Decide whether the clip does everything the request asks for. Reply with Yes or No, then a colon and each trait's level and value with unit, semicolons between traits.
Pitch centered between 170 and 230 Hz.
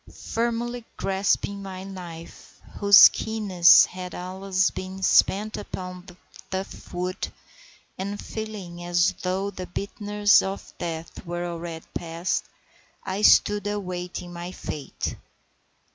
Yes: medium, 185 Hz